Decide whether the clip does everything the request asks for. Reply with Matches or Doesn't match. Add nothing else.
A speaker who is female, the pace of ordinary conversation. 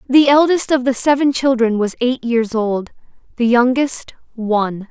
Matches